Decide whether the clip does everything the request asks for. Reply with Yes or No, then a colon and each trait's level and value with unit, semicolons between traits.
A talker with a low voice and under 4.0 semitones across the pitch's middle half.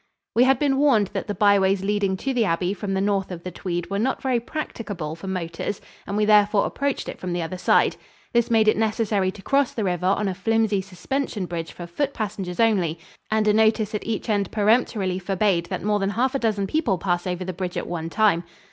No: high, 200 Hz; average, 3.2 semitones